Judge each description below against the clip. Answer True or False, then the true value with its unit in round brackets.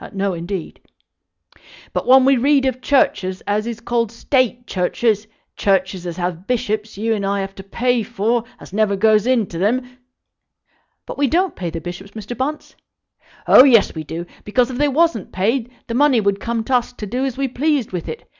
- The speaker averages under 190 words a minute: False (195 wpm)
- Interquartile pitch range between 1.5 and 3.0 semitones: False (4.5 semitones)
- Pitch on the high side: True (225 Hz)